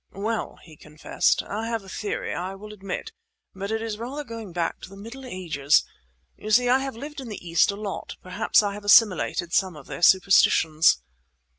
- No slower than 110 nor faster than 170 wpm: No, average, 195 wpm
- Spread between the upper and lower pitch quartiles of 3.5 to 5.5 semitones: Yes, average, 4.1 semitones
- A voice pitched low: No, high, 200 Hz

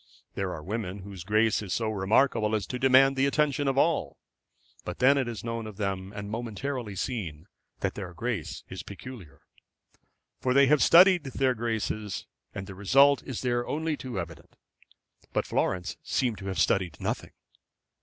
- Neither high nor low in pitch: No, low, 110 Hz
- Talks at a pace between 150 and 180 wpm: Yes, average, 165 wpm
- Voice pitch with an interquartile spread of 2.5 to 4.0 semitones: No, average, 5.3 semitones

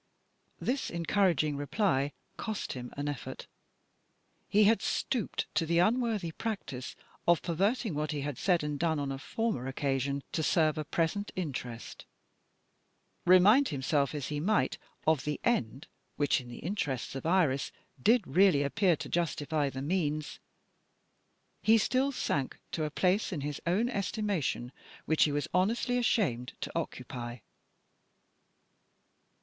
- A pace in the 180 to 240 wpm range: No, average, 140 wpm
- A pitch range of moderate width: No, wide, 6.1 semitones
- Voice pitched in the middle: Yes, medium, 160 Hz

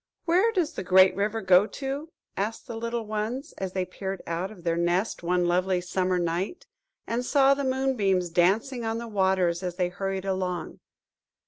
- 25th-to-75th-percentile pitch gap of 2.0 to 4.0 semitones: No, average, 4.5 semitones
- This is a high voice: Yes, high, 195 Hz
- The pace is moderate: Yes, average, 180 wpm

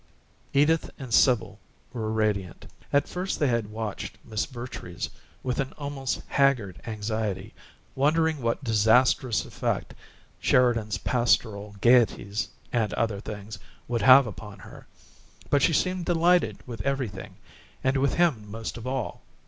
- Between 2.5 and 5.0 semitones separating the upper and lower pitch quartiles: Yes, average, 4.3 semitones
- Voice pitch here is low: Yes, low, 120 Hz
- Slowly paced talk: Yes, slow, 130 wpm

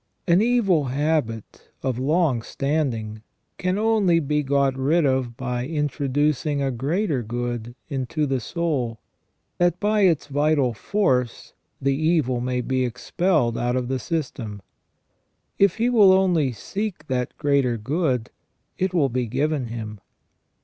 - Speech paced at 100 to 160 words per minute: Yes, average, 140 wpm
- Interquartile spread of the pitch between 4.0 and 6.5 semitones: Yes, average, 5.1 semitones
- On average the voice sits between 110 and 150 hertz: Yes, medium, 140 Hz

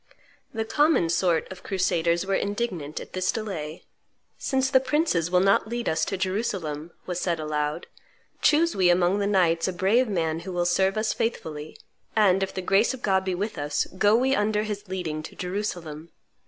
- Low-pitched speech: No, high, 190 Hz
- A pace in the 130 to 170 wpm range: No, average, 185 wpm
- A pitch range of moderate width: Yes, average, 4.0 semitones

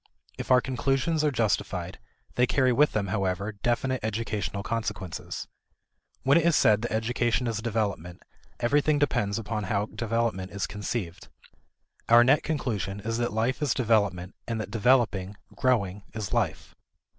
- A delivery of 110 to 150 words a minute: Yes, average, 145 wpm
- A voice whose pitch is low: Yes, low, 115 Hz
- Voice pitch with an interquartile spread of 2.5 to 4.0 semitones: Yes, average, 3.7 semitones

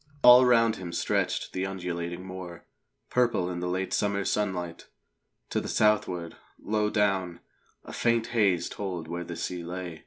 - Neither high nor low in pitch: No, very low, 95 Hz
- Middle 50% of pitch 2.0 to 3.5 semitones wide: Yes, average, 3.2 semitones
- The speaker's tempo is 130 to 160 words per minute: Yes, average, 155 wpm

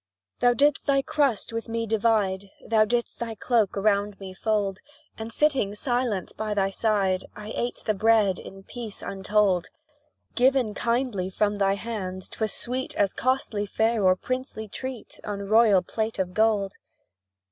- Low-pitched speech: No, high, 215 Hz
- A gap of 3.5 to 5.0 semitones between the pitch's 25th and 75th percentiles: No, average, 3.1 semitones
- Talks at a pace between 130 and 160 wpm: Yes, average, 155 wpm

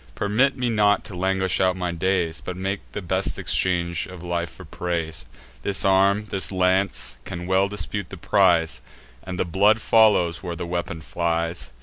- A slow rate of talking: No, average, 175 wpm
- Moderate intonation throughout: No, narrow, 2.3 semitones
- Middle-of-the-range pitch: No, very low, 95 Hz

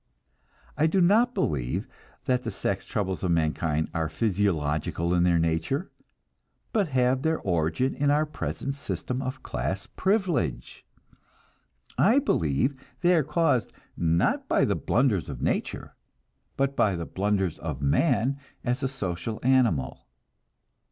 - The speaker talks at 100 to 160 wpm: Yes, slow, 135 wpm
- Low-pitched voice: Yes, low, 115 Hz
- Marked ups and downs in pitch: Yes, wide, 9.0 semitones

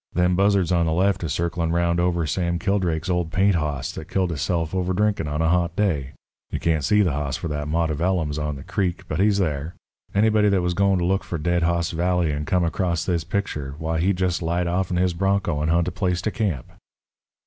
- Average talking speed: No, fast, 230 wpm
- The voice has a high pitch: No, very low, 85 Hz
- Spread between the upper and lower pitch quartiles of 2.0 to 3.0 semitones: Yes, narrow, 2.6 semitones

